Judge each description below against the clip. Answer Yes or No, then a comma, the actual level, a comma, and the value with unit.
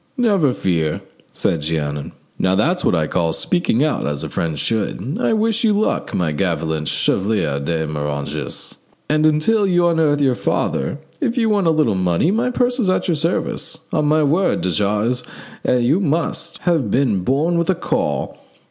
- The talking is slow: No, average, 175 wpm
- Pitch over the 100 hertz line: Yes, medium, 140 Hz